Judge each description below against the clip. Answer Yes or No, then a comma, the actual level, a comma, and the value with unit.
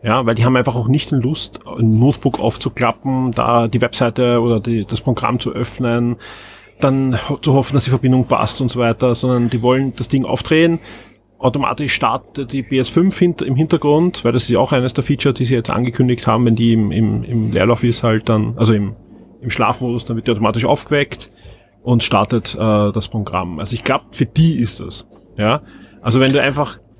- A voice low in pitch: Yes, low, 120 Hz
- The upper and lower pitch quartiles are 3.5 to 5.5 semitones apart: No, average, 2.8 semitones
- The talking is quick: Yes, fast, 200 wpm